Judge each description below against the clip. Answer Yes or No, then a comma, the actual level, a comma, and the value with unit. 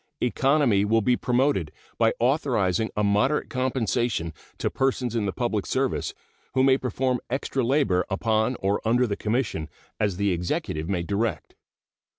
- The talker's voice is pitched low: Yes, low, 115 Hz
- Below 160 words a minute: Yes, average, 150 wpm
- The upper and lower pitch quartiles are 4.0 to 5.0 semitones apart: Yes, average, 4.3 semitones